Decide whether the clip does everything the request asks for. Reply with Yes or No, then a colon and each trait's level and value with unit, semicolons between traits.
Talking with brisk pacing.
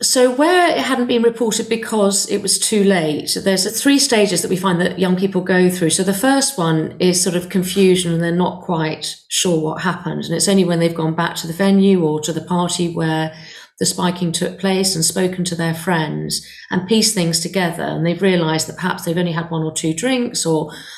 Yes: fast, 225 wpm